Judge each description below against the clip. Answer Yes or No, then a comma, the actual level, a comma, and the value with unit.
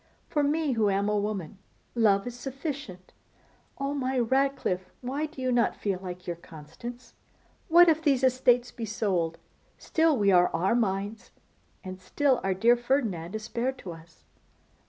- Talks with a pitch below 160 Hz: No, high, 235 Hz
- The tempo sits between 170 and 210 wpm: No, average, 155 wpm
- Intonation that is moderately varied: No, wide, 5.8 semitones